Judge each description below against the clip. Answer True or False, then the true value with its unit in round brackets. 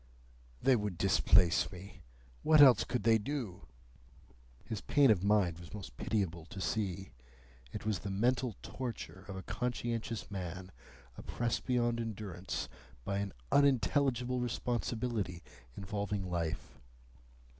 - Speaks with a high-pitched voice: False (105 Hz)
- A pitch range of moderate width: True (4.2 semitones)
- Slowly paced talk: True (125 wpm)